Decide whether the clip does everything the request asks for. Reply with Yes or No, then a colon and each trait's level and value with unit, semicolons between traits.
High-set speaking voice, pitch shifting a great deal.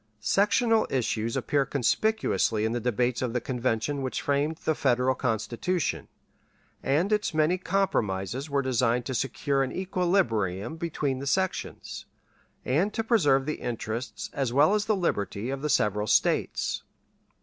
No: low, 135 Hz; wide, 6.3 semitones